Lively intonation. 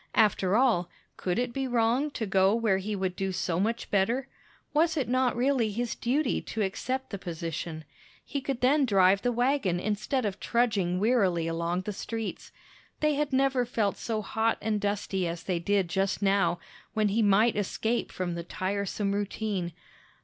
No: average, 4.5 semitones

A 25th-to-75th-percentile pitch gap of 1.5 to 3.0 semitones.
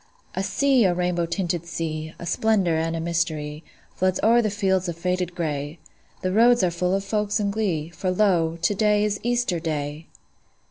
No: average, 3.8 semitones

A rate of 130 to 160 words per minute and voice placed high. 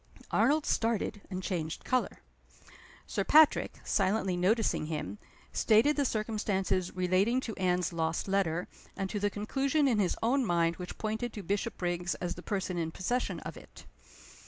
Yes: average, 155 wpm; high, 195 Hz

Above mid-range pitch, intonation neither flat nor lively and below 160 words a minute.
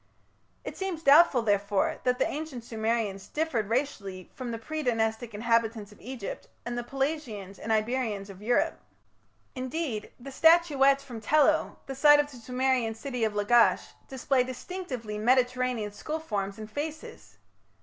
Yes: high, 245 Hz; average, 4.1 semitones; average, 150 wpm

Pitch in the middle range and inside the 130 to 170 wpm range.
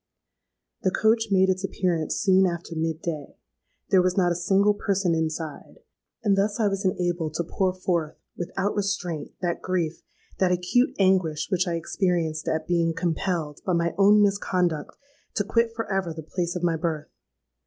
Yes: medium, 180 Hz; average, 165 wpm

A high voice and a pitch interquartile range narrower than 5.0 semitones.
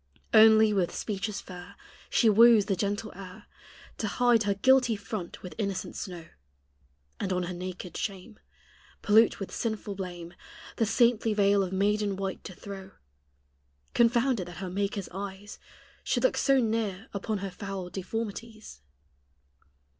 Yes: high, 200 Hz; narrow, 2.6 semitones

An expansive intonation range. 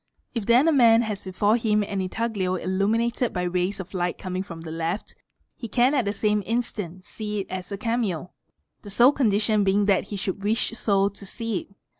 No: average, 3.4 semitones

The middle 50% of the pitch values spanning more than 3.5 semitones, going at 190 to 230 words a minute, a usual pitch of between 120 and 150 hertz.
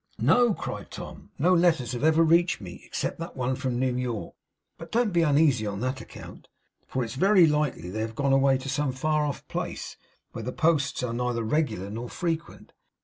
Yes: average, 4.8 semitones; average, 200 wpm; low, 135 Hz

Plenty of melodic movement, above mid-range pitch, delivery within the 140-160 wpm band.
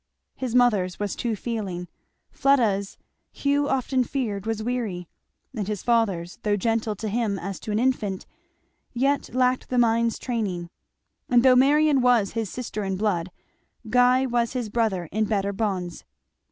No: average, 3.8 semitones; high, 225 Hz; average, 155 wpm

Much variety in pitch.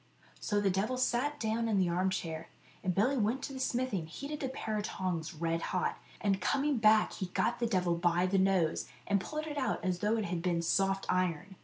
No: average, 4.7 semitones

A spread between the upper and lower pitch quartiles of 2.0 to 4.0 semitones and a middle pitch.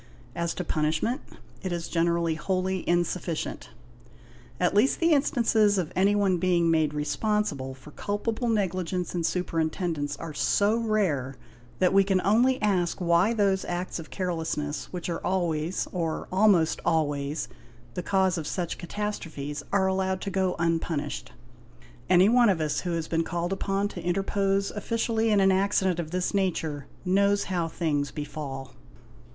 Yes: average, 3.4 semitones; medium, 180 Hz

